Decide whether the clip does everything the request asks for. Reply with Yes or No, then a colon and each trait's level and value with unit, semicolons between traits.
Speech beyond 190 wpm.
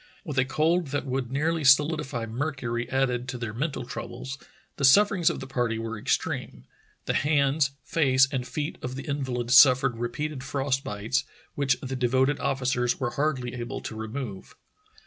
No: average, 165 wpm